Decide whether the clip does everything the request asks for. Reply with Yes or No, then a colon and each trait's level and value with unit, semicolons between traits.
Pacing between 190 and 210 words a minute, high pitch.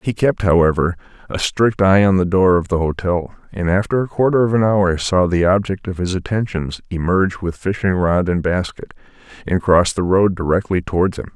No: average, 200 wpm; very low, 95 Hz